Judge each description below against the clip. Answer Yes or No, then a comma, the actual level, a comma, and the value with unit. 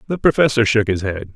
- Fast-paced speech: Yes, fast, 220 wpm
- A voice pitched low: Yes, low, 120 Hz